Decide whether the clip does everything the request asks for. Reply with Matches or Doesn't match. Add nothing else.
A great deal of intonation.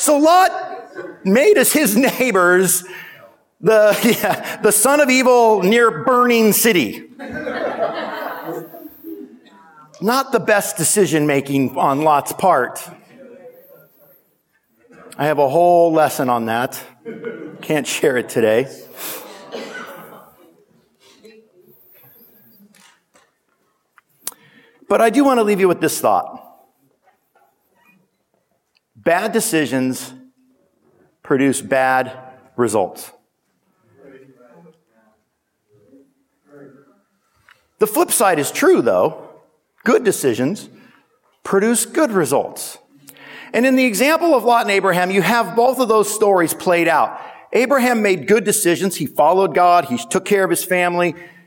Matches